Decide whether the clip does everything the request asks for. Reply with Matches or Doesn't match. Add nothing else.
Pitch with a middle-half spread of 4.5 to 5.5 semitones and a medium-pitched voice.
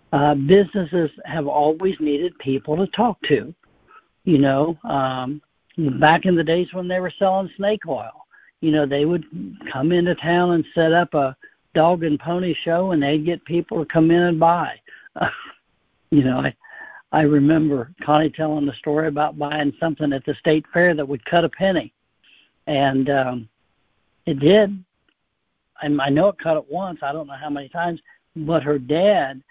Doesn't match